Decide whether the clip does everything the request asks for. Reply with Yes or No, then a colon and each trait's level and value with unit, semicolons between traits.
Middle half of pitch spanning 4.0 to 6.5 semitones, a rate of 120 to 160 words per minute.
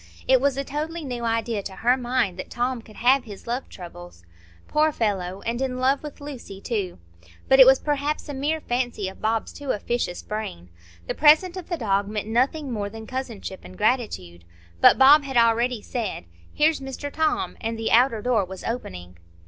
No: average, 4.6 semitones; average, 190 wpm